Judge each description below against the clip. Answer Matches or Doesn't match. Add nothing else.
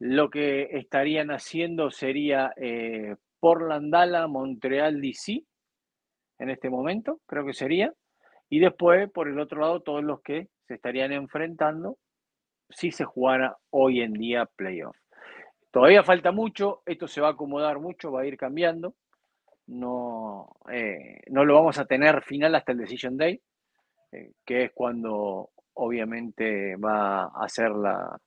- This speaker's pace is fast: Doesn't match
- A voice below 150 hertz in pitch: Matches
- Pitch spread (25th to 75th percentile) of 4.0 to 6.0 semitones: Matches